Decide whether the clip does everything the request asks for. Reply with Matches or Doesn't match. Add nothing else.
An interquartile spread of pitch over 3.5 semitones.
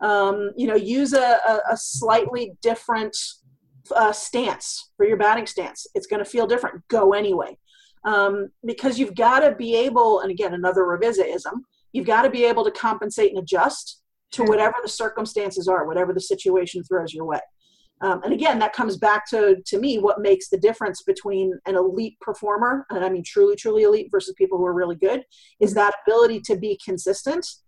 Matches